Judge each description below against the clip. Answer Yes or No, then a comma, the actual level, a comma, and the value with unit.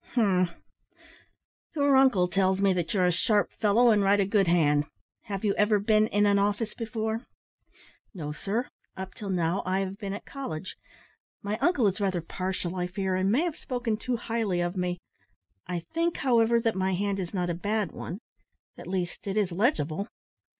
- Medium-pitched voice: No, high, 200 Hz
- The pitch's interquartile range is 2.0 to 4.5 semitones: Yes, average, 3.3 semitones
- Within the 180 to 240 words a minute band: Yes, average, 185 wpm